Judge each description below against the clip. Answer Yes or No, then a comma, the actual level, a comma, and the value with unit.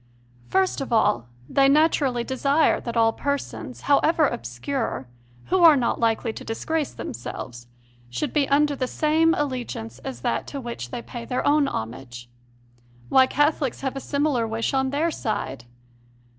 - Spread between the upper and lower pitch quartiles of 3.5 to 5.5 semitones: Yes, average, 4.7 semitones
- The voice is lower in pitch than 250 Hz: No, very high, 260 Hz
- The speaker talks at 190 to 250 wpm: No, average, 155 wpm